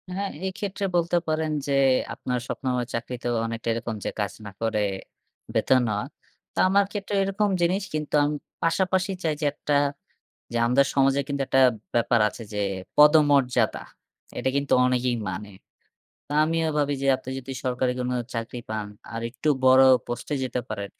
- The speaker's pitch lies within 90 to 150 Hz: Yes, low, 135 Hz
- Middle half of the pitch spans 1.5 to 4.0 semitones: No, average, 4.8 semitones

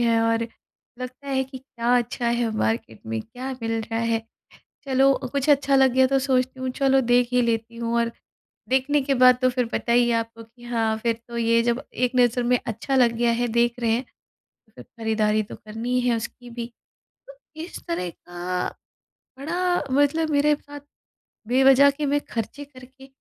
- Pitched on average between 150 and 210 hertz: No, high, 245 Hz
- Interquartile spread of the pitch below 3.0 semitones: Yes, narrow, 2.6 semitones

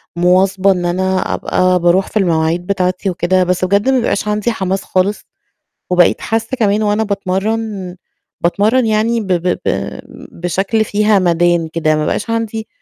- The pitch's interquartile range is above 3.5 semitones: No, average, 3.1 semitones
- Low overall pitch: No, high, 190 Hz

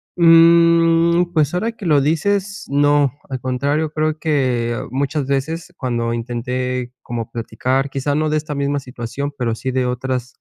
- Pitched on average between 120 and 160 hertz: Yes, medium, 140 Hz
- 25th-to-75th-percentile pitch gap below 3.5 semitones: No, average, 4.0 semitones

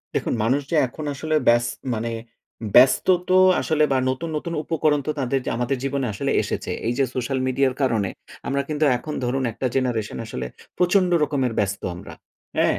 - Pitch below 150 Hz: Yes, low, 135 Hz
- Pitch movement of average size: Yes, average, 3.9 semitones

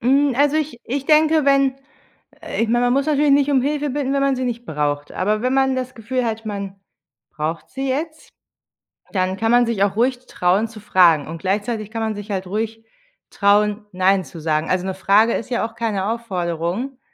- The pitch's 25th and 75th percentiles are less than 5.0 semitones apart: No, wide, 5.5 semitones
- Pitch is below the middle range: No, high, 225 Hz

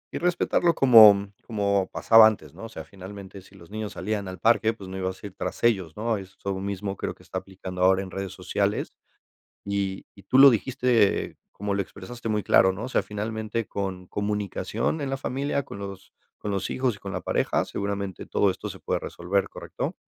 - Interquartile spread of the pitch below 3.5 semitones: Yes, average, 2.7 semitones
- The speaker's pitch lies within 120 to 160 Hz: No, low, 100 Hz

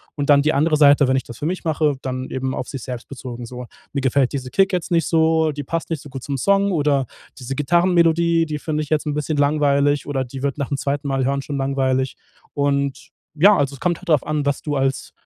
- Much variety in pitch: No, narrow, 2.6 semitones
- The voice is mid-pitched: Yes, medium, 145 Hz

